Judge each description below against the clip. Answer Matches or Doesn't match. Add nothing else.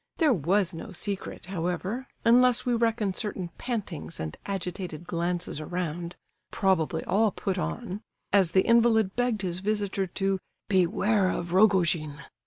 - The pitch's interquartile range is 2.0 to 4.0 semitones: Matches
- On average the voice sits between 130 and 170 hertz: Doesn't match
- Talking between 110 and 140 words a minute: Matches